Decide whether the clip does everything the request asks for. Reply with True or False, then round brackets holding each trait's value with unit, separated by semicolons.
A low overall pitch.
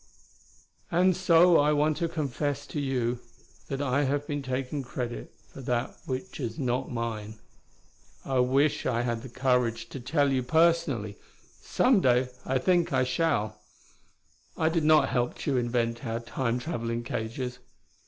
True (130 Hz)